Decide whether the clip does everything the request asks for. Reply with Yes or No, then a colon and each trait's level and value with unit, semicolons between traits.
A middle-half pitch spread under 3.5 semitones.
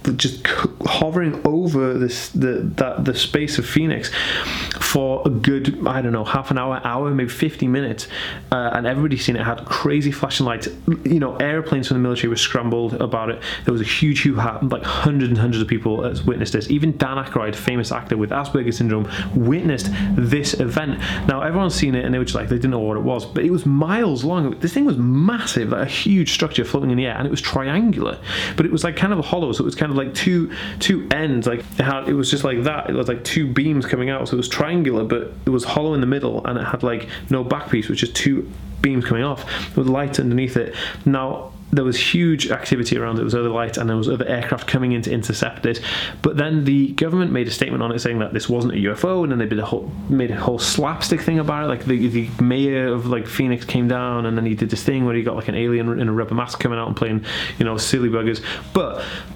No: average, 3.9 semitones